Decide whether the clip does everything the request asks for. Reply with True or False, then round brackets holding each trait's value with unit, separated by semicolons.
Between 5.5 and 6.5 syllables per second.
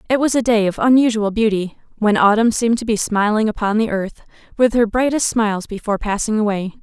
True (6.0 syllables/s)